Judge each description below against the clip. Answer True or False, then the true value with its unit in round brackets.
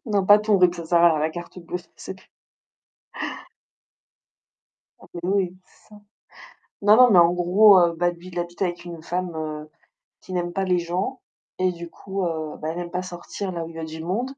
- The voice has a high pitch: False (175 Hz)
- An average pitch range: False (1.8 semitones)